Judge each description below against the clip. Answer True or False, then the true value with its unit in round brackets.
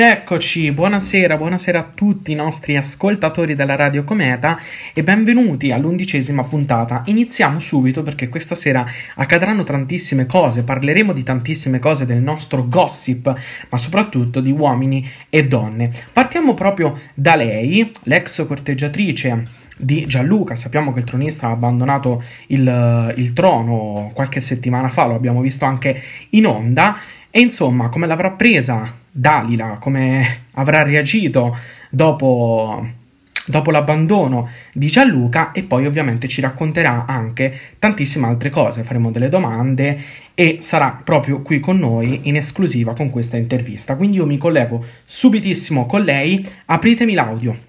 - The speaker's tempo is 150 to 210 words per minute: False (135 wpm)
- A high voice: False (140 Hz)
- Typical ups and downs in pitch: True (4.9 semitones)